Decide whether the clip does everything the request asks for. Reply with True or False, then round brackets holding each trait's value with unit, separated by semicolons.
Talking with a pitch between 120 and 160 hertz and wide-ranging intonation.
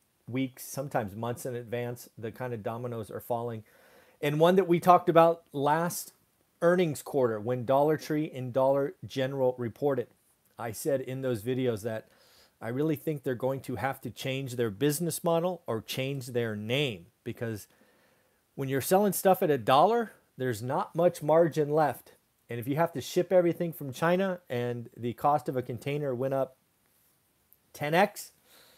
False (135 Hz; 4.9 semitones)